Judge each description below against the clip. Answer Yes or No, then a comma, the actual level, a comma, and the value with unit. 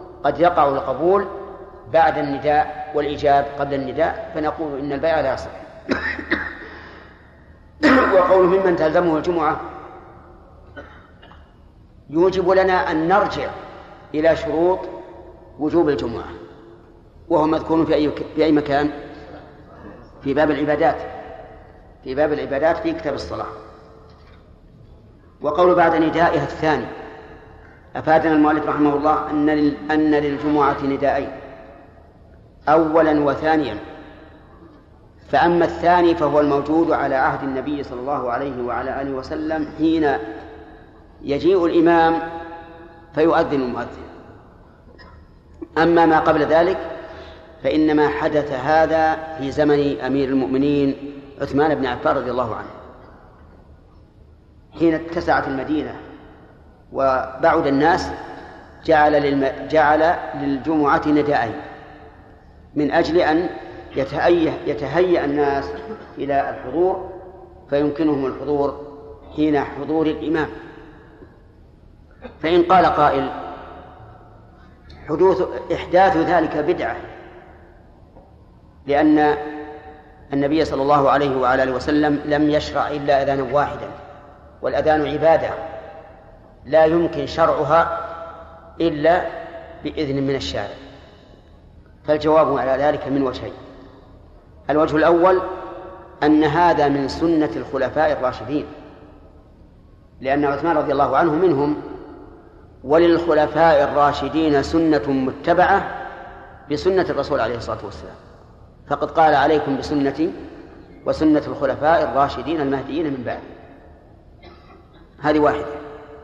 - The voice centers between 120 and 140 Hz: No, medium, 150 Hz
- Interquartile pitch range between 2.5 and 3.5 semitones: Yes, average, 3.0 semitones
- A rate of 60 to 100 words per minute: Yes, average, 90 wpm